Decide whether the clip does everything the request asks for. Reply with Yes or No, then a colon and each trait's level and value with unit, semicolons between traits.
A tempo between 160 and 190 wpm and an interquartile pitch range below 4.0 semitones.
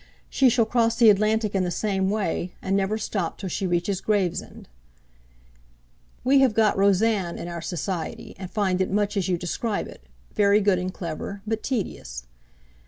Yes: average, 170 wpm; average, 2.9 semitones